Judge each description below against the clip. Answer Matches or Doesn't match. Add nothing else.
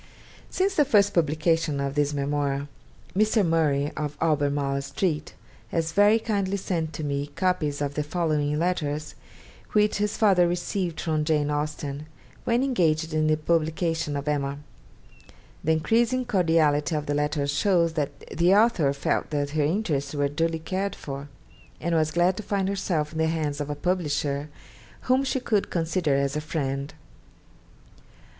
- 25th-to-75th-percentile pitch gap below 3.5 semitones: Doesn't match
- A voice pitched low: Doesn't match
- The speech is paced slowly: Doesn't match